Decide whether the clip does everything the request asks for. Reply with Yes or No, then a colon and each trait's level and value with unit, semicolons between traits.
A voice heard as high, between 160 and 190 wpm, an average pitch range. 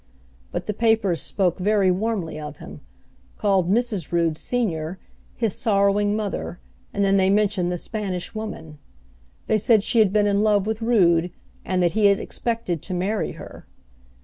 Yes: high, 200 Hz; average, 165 wpm; average, 3.2 semitones